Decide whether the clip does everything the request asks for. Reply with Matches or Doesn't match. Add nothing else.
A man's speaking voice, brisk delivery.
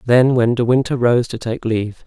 Matches